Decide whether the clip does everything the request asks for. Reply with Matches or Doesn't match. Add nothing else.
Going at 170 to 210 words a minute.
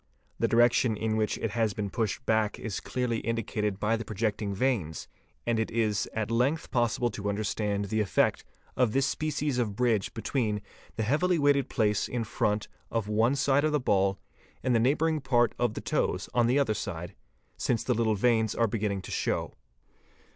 Matches